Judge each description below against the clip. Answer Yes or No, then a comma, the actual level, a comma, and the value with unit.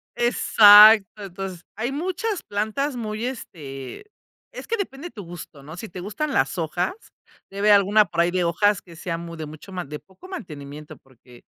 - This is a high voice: Yes, high, 195 Hz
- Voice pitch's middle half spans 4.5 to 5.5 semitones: Yes, average, 5.1 semitones